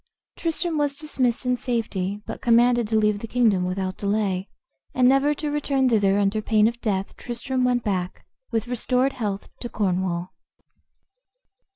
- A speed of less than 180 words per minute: Yes, average, 155 wpm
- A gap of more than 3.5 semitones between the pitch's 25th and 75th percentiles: Yes, average, 4.1 semitones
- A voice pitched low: No, high, 230 Hz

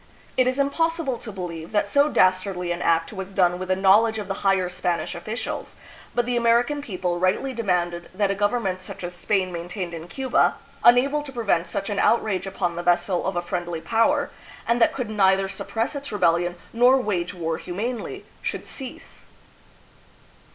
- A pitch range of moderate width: Yes, average, 5.0 semitones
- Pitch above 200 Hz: No, high, 195 Hz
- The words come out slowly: No, average, 180 wpm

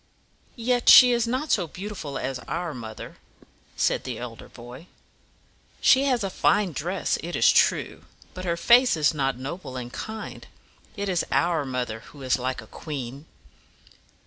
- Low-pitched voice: No, medium, 165 Hz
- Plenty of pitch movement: Yes, wide, 8.1 semitones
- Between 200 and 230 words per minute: No, average, 160 wpm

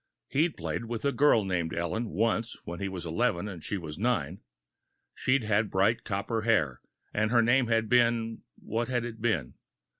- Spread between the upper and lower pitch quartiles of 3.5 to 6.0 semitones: Yes, average, 4.1 semitones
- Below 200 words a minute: Yes, average, 180 wpm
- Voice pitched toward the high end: No, low, 110 Hz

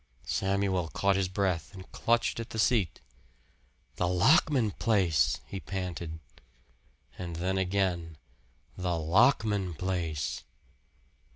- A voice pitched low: Yes, very low, 95 Hz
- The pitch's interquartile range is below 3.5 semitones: Yes, narrow, 2.5 semitones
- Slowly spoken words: Yes, slow, 105 wpm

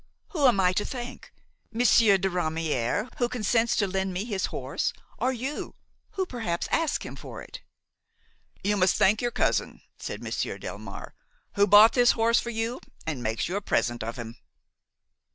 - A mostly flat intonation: No, average, 5.0 semitones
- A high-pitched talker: Yes, high, 205 Hz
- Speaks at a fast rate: No, average, 170 wpm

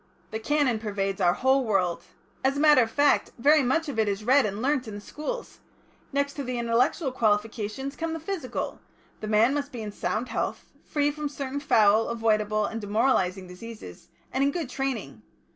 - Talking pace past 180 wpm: Yes, average, 190 wpm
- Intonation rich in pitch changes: No, average, 4.9 semitones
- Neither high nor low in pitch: No, high, 245 Hz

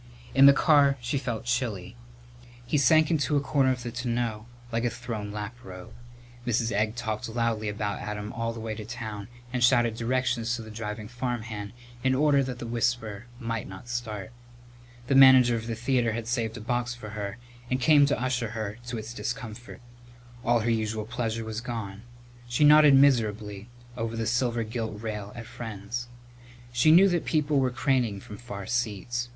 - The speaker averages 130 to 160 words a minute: No, average, 180 wpm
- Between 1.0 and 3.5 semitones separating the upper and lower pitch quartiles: Yes, narrow, 2.5 semitones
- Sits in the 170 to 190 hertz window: No, low, 120 Hz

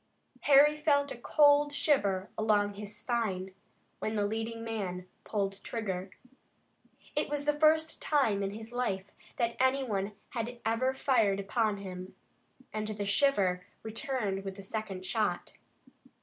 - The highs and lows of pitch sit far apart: No, average, 4.8 semitones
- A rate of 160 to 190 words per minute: No, average, 140 wpm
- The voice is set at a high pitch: Yes, high, 220 Hz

